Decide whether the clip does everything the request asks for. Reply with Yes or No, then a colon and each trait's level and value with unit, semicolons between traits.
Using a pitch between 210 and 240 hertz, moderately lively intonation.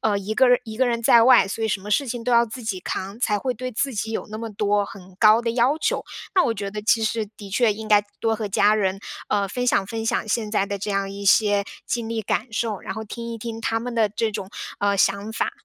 No: high, 220 Hz; narrow, 2.3 semitones